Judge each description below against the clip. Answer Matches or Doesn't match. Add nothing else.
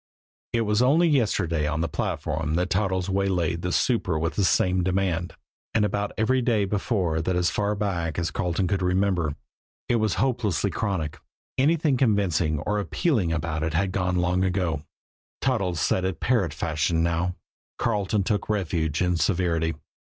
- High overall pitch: Doesn't match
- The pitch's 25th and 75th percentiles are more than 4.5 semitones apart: Doesn't match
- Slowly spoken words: Doesn't match